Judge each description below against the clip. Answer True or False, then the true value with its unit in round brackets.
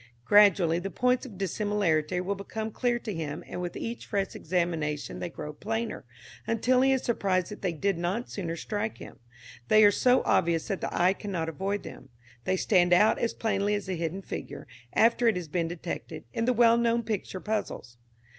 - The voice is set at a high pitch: True (195 Hz)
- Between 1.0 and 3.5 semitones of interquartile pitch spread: False (4.3 semitones)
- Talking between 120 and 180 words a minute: False (195 wpm)